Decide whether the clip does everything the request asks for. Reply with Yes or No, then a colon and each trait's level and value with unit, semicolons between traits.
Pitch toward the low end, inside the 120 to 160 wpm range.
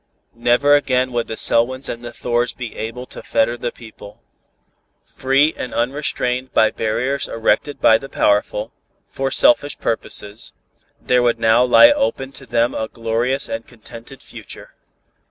Yes: low, 120 Hz; average, 150 wpm